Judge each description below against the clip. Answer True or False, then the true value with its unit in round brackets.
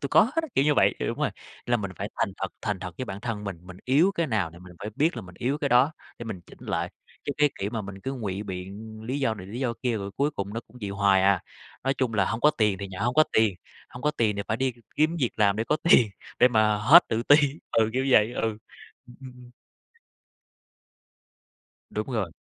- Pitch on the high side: False (110 Hz)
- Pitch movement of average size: True (4.7 semitones)